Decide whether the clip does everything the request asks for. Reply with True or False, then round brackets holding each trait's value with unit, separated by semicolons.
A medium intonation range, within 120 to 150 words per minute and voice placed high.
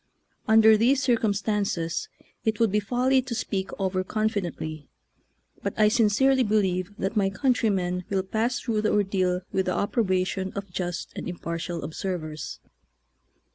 True (3.2 semitones; 140 wpm; 200 Hz)